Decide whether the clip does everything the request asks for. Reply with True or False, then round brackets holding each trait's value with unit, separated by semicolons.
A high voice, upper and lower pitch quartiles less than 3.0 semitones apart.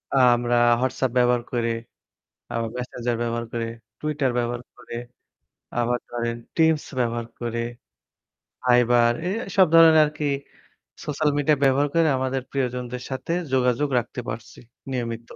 False (125 Hz; 2.4 semitones)